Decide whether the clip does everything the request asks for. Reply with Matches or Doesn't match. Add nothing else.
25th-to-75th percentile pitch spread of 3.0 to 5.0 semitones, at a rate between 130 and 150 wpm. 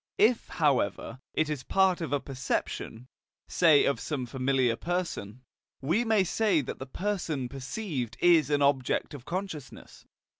Doesn't match